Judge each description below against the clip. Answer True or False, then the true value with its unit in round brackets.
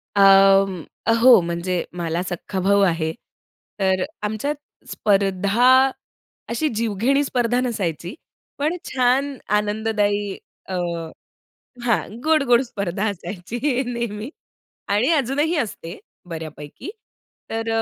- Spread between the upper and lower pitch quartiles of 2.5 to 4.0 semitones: False (4.7 semitones)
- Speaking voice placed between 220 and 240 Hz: False (210 Hz)